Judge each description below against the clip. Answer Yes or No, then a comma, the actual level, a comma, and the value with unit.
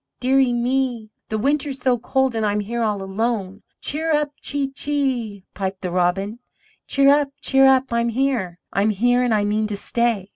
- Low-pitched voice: No, high, 235 Hz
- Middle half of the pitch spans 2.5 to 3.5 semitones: No, average, 4.5 semitones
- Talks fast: No, average, 175 wpm